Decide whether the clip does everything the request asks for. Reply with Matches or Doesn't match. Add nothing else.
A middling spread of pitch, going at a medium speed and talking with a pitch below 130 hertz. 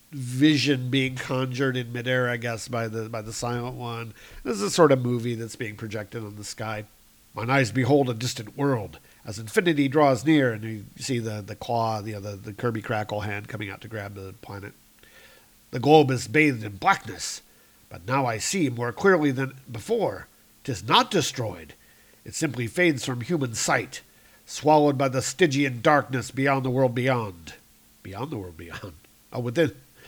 Matches